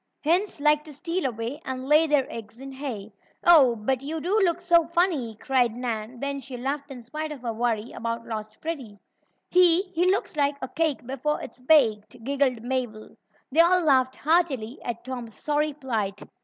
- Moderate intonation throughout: Yes, average, 4.7 semitones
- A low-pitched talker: No, very high, 270 Hz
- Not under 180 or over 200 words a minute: Yes, average, 185 wpm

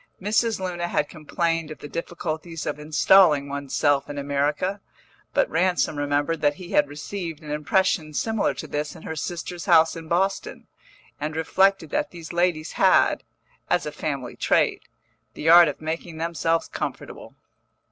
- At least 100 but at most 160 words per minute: Yes, average, 155 wpm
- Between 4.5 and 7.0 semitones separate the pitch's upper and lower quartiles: No, average, 2.9 semitones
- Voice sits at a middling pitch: Yes, medium, 165 Hz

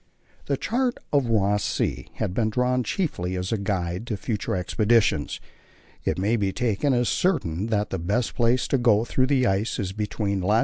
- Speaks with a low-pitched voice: Yes, low, 110 Hz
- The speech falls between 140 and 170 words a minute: No, average, 185 wpm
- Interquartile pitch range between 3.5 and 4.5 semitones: Yes, average, 4.2 semitones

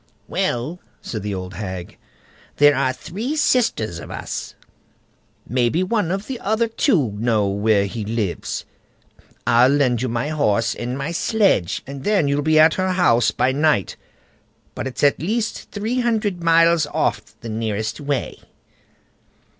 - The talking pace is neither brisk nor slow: Yes, average, 145 wpm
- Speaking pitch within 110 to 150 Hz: Yes, medium, 140 Hz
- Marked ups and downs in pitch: Yes, wide, 8.6 semitones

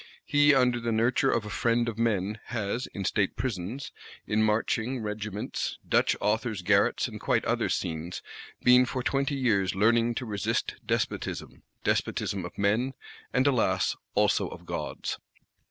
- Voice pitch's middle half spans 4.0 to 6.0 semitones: No, average, 3.6 semitones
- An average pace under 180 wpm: Yes, average, 150 wpm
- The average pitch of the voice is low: Yes, low, 110 Hz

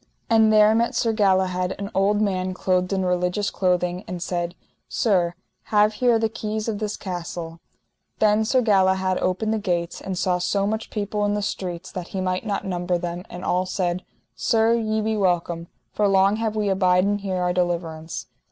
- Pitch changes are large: No, average, 2.8 semitones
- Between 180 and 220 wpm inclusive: Yes, average, 185 wpm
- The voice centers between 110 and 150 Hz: No, high, 190 Hz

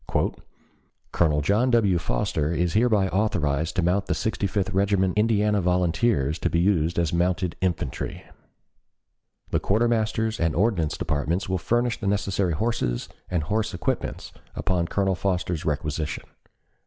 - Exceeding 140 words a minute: No, slow, 135 wpm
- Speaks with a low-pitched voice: Yes, very low, 95 Hz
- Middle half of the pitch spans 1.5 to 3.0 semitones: No, average, 4.0 semitones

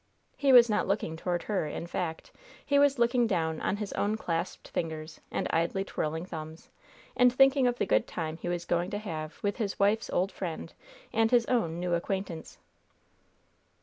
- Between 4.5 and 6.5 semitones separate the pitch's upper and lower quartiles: Yes, wide, 5.4 semitones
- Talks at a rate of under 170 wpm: No, average, 180 wpm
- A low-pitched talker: No, high, 190 Hz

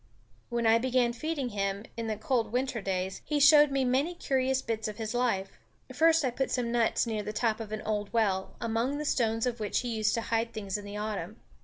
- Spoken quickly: Yes, fast, 225 wpm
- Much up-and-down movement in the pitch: No, average, 3.2 semitones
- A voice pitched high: Yes, high, 230 Hz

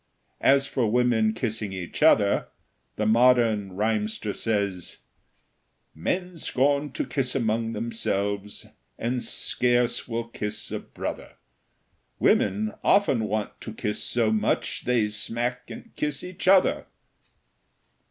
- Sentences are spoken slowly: Yes, slow, 115 wpm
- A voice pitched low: Yes, low, 115 Hz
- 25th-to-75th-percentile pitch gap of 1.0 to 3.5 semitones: Yes, average, 2.9 semitones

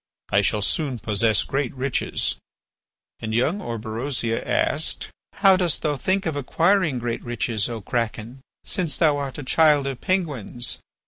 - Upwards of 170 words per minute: No, average, 145 wpm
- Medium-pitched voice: No, low, 130 Hz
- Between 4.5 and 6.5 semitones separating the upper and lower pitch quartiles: Yes, average, 5.2 semitones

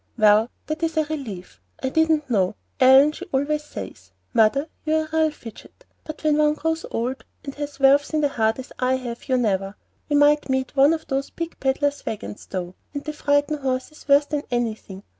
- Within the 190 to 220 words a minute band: Yes, average, 195 wpm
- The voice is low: No, very high, 280 Hz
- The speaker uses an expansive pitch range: No, average, 4.2 semitones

